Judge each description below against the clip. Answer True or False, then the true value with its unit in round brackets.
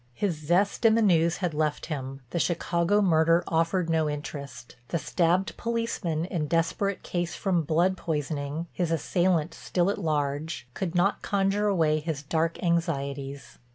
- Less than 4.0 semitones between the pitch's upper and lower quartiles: True (3.2 semitones)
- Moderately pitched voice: True (165 Hz)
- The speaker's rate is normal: True (150 wpm)